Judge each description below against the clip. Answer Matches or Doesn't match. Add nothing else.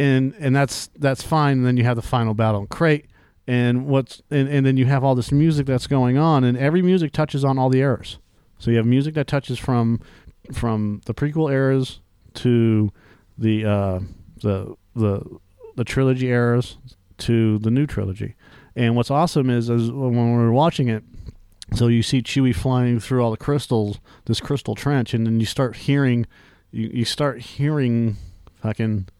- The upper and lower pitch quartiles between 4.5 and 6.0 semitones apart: Doesn't match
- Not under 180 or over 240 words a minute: Matches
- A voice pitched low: Matches